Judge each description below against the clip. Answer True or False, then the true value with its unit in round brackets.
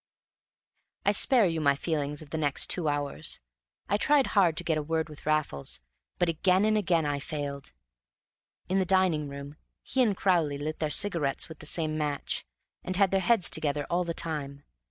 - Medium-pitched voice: True (160 Hz)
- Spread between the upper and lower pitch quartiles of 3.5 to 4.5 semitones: True (4.1 semitones)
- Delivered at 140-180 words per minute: False (190 wpm)